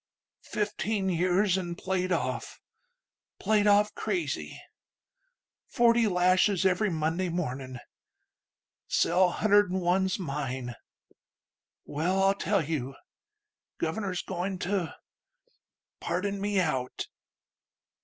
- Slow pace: Yes, slow, 90 wpm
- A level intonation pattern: No, average, 3.3 semitones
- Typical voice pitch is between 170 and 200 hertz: Yes, medium, 185 Hz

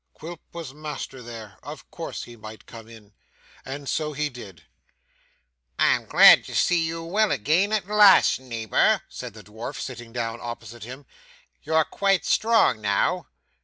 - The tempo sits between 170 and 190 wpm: No, average, 155 wpm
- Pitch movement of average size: No, wide, 6.4 semitones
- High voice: No, low, 130 Hz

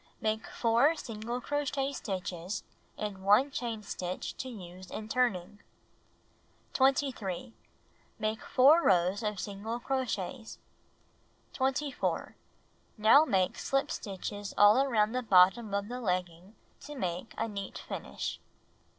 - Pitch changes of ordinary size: Yes, average, 4.8 semitones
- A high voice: Yes, high, 215 Hz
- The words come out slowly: Yes, slow, 115 wpm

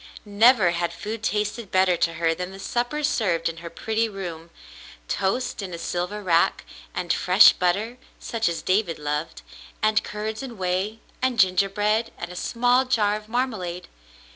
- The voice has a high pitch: Yes, high, 200 Hz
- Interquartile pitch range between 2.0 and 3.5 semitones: No, average, 4.1 semitones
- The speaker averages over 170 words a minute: No, average, 165 wpm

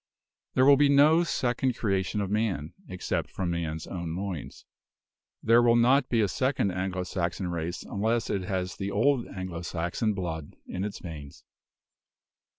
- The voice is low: Yes, very low, 95 Hz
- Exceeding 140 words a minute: Yes, average, 155 wpm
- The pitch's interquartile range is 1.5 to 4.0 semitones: No, average, 5.2 semitones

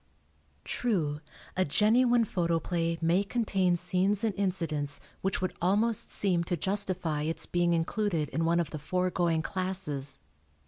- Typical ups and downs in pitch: Yes, average, 3.2 semitones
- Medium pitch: Yes, medium, 180 Hz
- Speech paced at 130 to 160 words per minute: Yes, average, 140 wpm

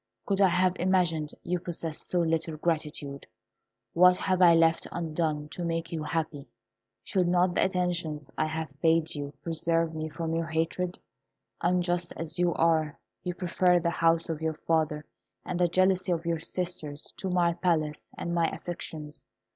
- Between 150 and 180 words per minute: Yes, average, 165 wpm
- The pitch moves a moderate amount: No, narrow, 2.0 semitones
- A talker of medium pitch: Yes, medium, 165 Hz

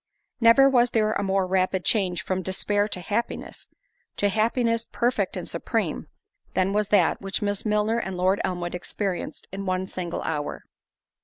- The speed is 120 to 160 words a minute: Yes, average, 150 wpm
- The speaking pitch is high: Yes, high, 195 Hz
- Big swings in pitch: No, average, 2.9 semitones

